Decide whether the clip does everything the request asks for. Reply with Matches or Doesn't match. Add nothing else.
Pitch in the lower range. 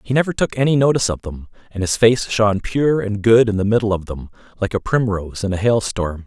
Matches